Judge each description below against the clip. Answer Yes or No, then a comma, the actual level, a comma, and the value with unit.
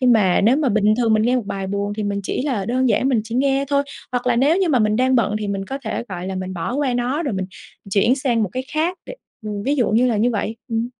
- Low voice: No, high, 235 Hz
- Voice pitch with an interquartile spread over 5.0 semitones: No, average, 4.1 semitones